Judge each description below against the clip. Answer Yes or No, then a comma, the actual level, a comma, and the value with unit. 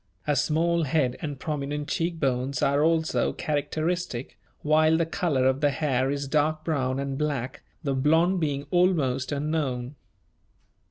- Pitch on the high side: No, medium, 145 Hz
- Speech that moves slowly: No, average, 145 wpm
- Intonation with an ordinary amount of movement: Yes, average, 3.0 semitones